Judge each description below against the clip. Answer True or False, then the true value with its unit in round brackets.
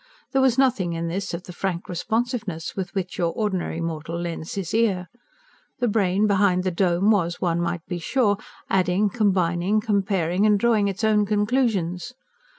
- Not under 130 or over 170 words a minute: True (165 wpm)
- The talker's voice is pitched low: False (190 Hz)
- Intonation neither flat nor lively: True (3.5 semitones)